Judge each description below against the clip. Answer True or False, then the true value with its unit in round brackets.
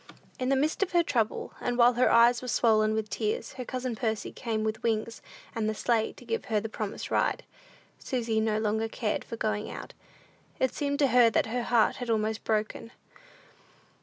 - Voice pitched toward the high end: True (225 Hz)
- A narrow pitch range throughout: True (2.3 semitones)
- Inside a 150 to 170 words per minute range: False (195 wpm)